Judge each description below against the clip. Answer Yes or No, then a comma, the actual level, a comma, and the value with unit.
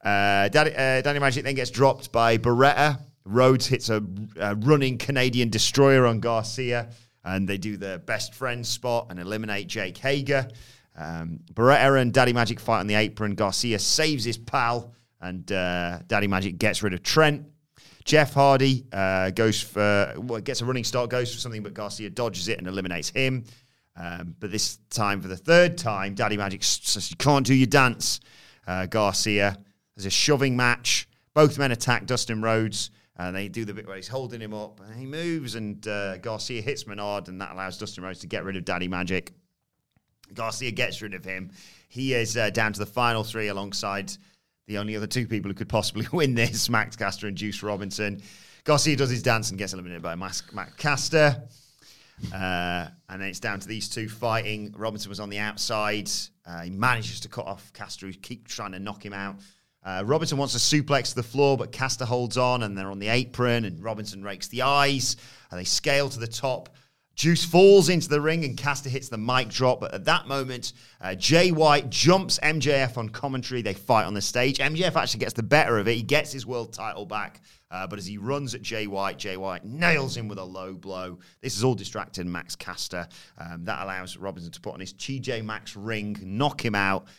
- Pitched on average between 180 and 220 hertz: No, low, 115 Hz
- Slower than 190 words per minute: No, fast, 205 wpm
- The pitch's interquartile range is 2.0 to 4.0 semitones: No, average, 4.6 semitones